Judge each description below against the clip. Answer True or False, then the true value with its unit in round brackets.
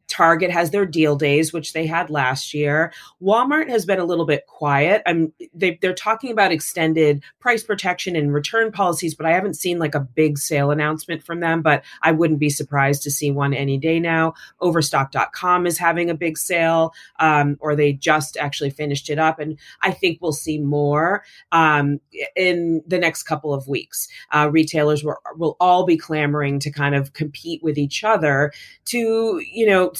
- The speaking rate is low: False (185 wpm)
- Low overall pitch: False (160 Hz)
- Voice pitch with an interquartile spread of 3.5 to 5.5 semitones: False (2.9 semitones)